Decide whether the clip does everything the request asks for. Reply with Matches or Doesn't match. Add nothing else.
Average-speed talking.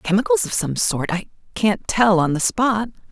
Matches